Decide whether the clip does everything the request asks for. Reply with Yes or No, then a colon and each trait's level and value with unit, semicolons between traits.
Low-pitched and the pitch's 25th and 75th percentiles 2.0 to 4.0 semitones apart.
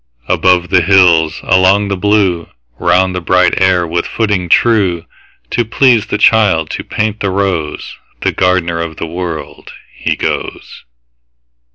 Yes: very low, 90 Hz; average, 3.2 semitones